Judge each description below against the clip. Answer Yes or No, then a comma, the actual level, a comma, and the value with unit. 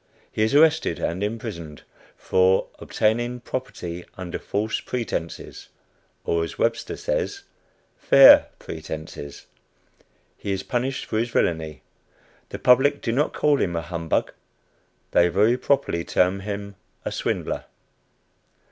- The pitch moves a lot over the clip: Yes, wide, 6.4 semitones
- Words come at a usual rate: No, slow, 120 wpm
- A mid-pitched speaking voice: No, low, 105 Hz